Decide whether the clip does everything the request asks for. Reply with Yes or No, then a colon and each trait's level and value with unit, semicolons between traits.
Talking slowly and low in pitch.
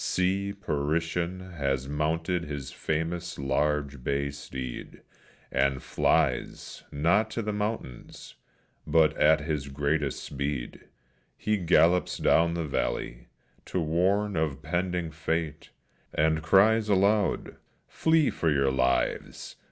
Yes: slow, 115 wpm; very low, 80 Hz